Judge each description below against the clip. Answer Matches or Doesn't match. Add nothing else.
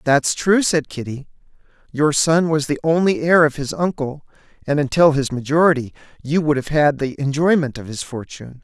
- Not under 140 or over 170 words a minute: Doesn't match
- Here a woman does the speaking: Doesn't match